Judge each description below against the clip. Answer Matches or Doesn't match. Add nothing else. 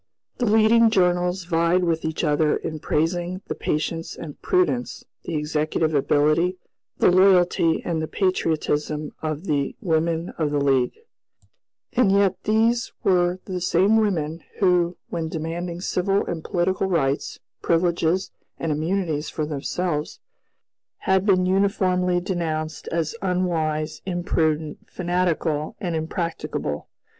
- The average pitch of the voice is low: Doesn't match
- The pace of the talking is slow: Matches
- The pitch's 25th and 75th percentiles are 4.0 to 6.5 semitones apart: Doesn't match